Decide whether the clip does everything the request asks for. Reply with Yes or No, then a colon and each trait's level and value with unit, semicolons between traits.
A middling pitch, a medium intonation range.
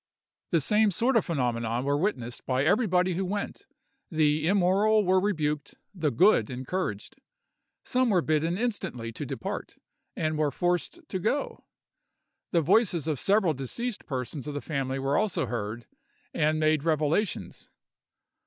No: medium, 160 Hz; wide, 6.3 semitones